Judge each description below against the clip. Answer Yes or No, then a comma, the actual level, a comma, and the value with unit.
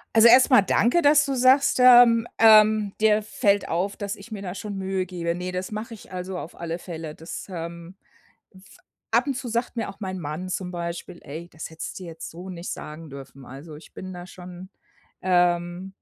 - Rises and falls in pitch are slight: No, average, 4.0 semitones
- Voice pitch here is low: No, medium, 185 Hz